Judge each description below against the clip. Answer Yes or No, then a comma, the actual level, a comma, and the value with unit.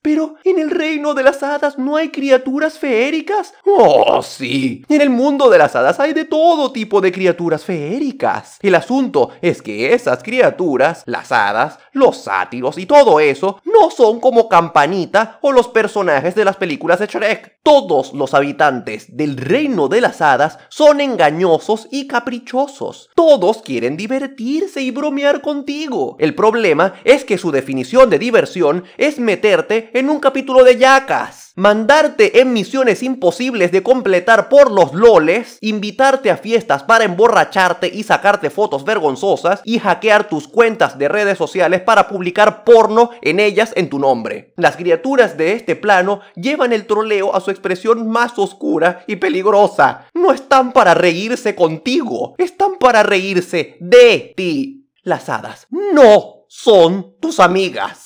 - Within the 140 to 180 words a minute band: Yes, average, 155 wpm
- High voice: Yes, high, 230 Hz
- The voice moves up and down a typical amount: No, wide, 6.8 semitones